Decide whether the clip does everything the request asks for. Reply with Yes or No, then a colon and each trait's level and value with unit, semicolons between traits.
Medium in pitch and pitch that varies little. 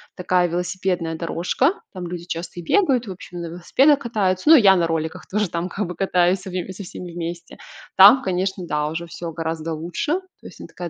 Yes: medium, 180 Hz; narrow, 2.3 semitones